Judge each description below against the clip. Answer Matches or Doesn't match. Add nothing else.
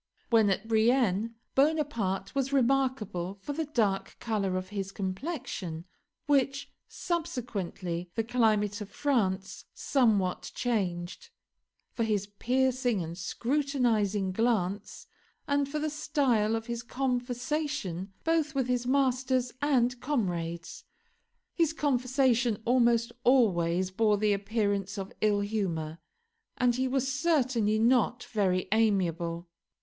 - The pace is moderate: Doesn't match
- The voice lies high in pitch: Matches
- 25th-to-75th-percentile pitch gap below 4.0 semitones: Doesn't match